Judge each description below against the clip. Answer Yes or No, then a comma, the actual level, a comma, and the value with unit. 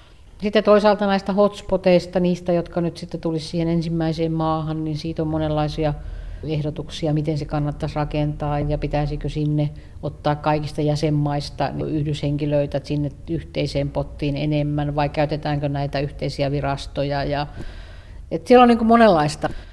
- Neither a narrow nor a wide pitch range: No, narrow, 2.1 semitones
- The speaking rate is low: No, average, 130 wpm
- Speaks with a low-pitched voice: No, medium, 150 Hz